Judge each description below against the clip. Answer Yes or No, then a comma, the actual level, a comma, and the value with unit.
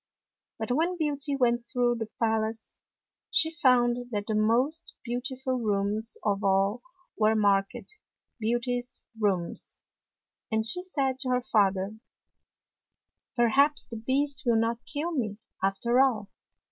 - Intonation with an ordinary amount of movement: Yes, average, 3.5 semitones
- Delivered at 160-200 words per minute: No, slow, 135 wpm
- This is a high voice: Yes, high, 240 Hz